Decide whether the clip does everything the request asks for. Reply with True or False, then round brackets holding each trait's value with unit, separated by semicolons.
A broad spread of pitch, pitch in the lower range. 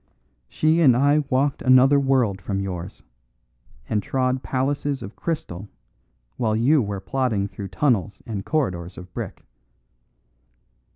True (5.8 semitones; 125 Hz)